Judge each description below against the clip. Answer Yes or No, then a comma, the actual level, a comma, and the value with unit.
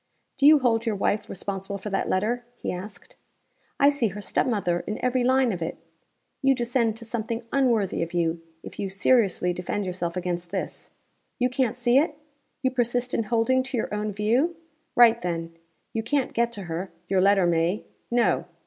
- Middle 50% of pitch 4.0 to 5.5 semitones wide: Yes, average, 4.7 semitones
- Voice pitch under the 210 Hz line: No, high, 220 Hz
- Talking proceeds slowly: No, average, 185 wpm